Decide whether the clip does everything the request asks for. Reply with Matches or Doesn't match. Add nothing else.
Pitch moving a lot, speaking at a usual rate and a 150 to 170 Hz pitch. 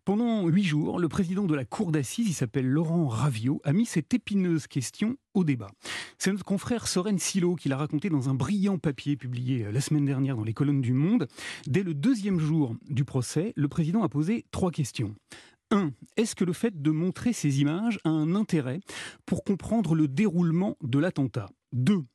Matches